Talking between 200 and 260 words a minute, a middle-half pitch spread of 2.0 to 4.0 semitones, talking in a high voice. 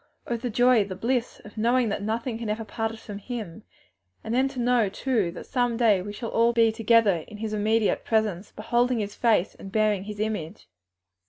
Yes: fast, 205 wpm; narrow, 2.4 semitones; high, 220 Hz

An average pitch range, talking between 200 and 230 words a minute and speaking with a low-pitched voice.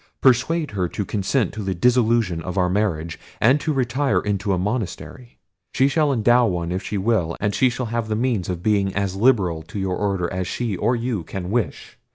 Yes: average, 4.8 semitones; fast, 205 wpm; low, 105 Hz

